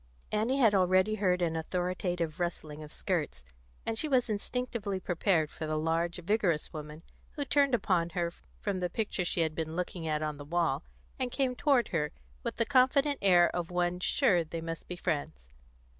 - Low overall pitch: No, medium, 180 Hz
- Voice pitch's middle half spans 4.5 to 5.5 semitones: Yes, average, 4.8 semitones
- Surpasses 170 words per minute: Yes, average, 185 wpm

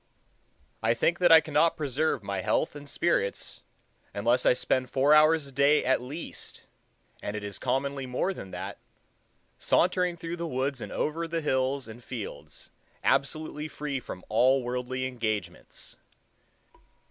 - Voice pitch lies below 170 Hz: Yes, low, 135 Hz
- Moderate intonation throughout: Yes, average, 3.9 semitones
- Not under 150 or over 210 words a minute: No, average, 140 wpm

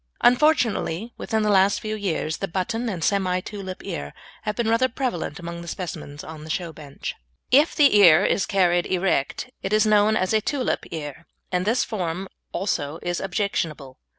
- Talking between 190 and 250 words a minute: No, average, 180 wpm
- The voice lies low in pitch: No, high, 190 Hz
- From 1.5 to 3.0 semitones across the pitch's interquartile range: No, average, 4.3 semitones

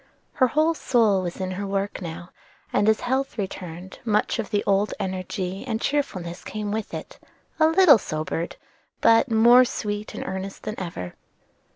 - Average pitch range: Yes, average, 4.1 semitones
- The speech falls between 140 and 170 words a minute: Yes, average, 165 wpm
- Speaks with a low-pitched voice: No, high, 205 Hz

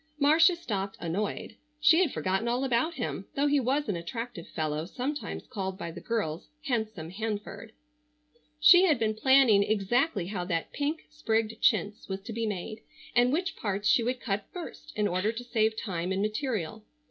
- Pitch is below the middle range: No, high, 220 Hz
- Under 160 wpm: No, average, 175 wpm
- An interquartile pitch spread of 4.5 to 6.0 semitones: Yes, average, 5.2 semitones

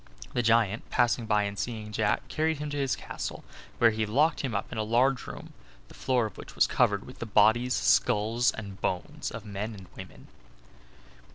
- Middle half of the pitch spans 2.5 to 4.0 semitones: Yes, average, 2.9 semitones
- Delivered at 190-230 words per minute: Yes, average, 195 wpm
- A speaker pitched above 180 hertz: No, low, 110 Hz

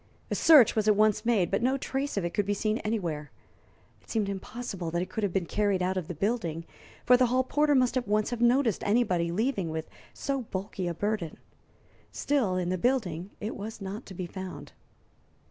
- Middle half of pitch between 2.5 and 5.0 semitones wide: Yes, average, 4.7 semitones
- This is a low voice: No, high, 205 Hz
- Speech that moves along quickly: Yes, fast, 210 wpm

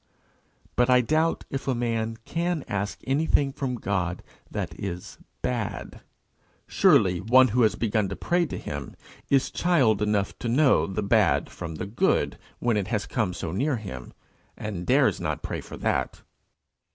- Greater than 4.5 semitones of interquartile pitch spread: Yes, average, 5.1 semitones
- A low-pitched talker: Yes, low, 115 Hz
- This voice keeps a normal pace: Yes, average, 165 wpm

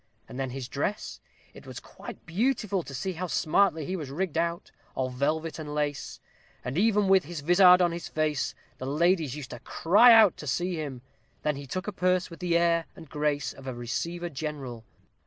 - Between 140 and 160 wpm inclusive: No, average, 200 wpm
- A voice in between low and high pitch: Yes, medium, 160 Hz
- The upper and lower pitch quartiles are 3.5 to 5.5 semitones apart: Yes, average, 4.3 semitones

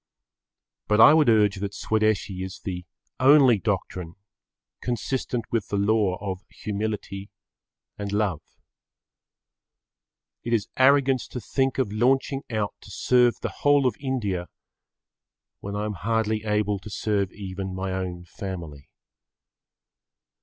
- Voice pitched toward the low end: Yes, low, 105 Hz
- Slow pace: Yes, slow, 130 wpm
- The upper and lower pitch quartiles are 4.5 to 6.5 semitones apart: No, average, 3.7 semitones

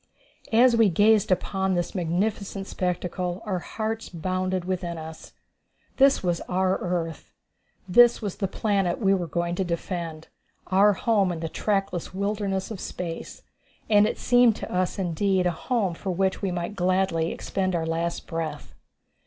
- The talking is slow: No, average, 155 wpm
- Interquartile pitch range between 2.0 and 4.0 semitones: Yes, average, 2.7 semitones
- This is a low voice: No, medium, 185 Hz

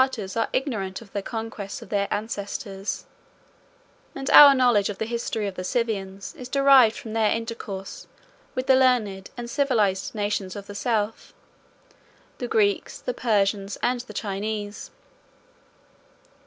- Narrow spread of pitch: No, average, 3.3 semitones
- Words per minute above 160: No, average, 155 wpm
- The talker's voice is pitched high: Yes, high, 215 Hz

